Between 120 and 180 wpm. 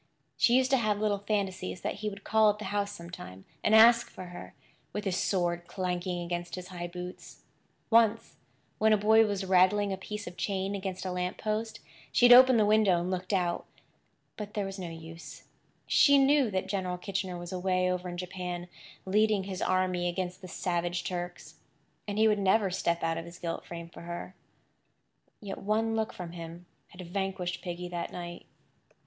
No: average, 190 wpm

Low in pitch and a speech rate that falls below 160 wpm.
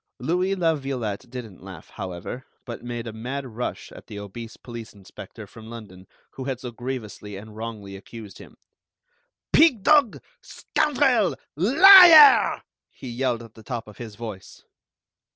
Yes: low, 120 Hz; average, 150 wpm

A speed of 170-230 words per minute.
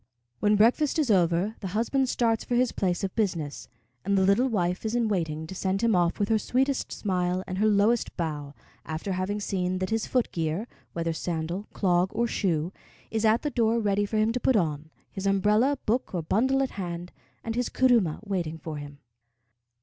Yes: average, 200 wpm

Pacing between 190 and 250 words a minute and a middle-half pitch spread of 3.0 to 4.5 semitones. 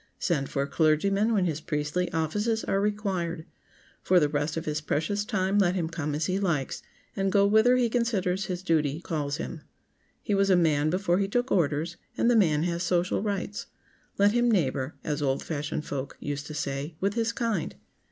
No: average, 195 wpm; average, 4.9 semitones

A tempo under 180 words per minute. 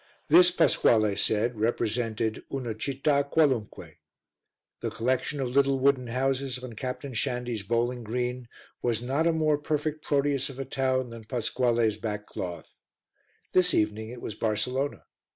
Yes: average, 140 wpm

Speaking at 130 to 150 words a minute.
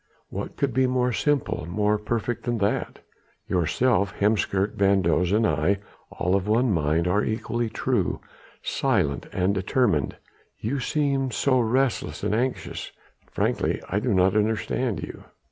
Yes: average, 145 wpm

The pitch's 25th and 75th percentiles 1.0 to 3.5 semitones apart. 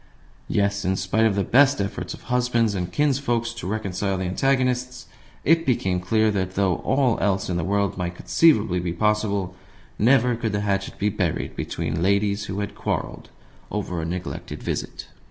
No: average, 4.1 semitones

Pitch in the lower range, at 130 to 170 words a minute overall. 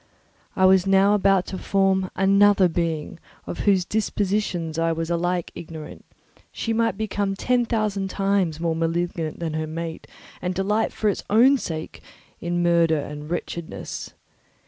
No: medium, 185 Hz; average, 145 wpm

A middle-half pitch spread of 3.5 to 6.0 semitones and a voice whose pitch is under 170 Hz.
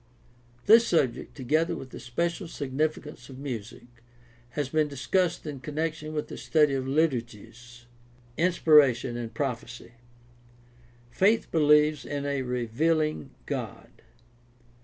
Yes: average, 4.3 semitones; medium, 140 Hz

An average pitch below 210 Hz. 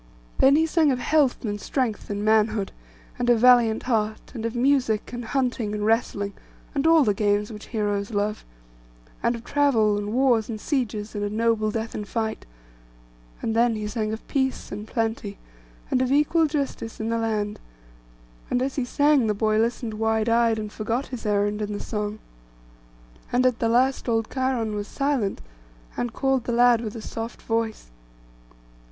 No: high, 225 Hz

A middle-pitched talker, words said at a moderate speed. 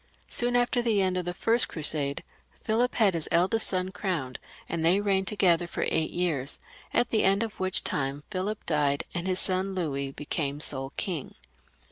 Yes: medium, 180 Hz; average, 185 wpm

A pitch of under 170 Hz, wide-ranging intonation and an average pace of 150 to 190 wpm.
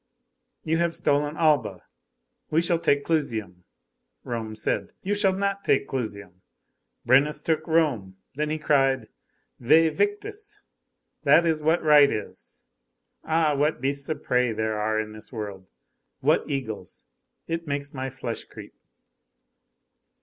No: medium, 140 Hz; wide, 6.4 semitones; slow, 135 wpm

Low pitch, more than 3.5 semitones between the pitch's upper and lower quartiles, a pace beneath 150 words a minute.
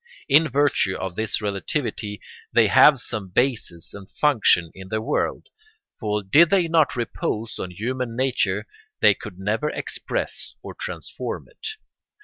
Yes: low, 110 Hz; wide, 5.6 semitones; average, 140 wpm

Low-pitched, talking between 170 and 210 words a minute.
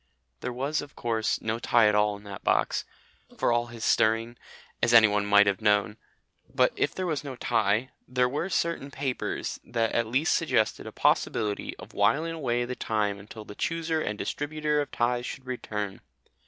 Yes: low, 120 Hz; average, 180 wpm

